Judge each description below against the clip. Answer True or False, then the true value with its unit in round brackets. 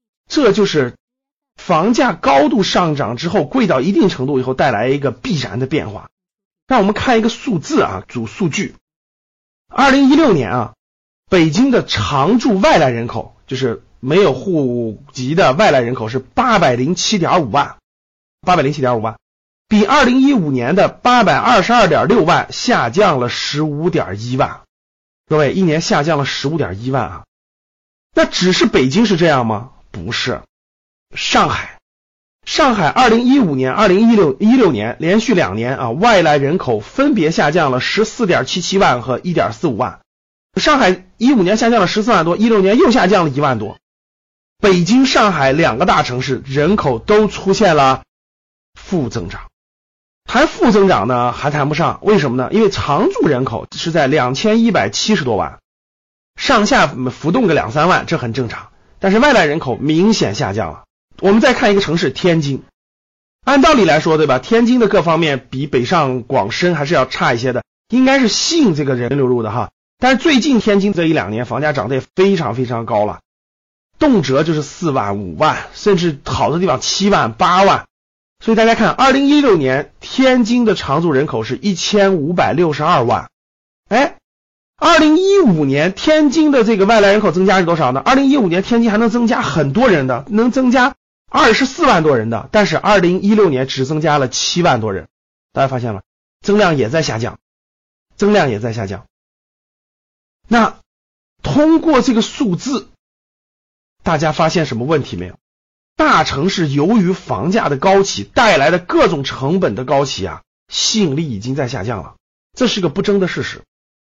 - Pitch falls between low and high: True (175 Hz)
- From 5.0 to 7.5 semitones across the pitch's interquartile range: False (8.9 semitones)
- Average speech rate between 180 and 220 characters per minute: False (265 characters per minute)